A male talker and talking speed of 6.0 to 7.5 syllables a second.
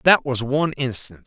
Yes: male; 6.3 syllables/s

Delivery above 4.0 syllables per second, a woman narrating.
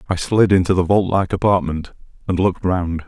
No: 5.6 syllables/s; male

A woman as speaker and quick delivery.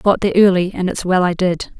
Yes: female; fast, 300 wpm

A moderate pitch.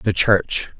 No: low, 100 Hz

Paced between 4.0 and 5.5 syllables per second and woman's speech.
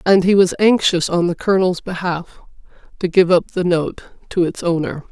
Yes: 5.2 syllables/s; female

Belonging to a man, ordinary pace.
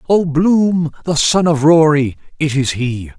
Yes: male; average, 150 wpm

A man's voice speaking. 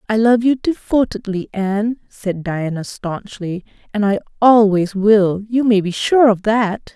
No: female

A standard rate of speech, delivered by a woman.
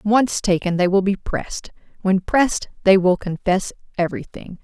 Yes: average, 155 wpm; female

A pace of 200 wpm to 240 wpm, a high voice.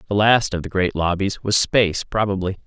No: fast, 205 wpm; very low, 95 Hz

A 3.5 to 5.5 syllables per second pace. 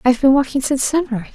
No: 8.5 syllables/s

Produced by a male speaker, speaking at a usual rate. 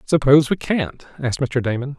Yes: male; average, 180 wpm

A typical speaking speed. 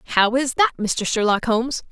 Yes: average, 190 wpm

